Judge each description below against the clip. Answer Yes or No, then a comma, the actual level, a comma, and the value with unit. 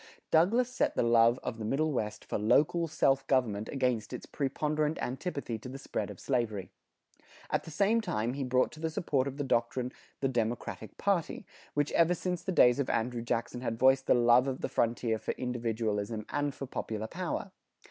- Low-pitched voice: Yes, low, 130 Hz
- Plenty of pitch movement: No, average, 4.5 semitones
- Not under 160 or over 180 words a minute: No, average, 190 wpm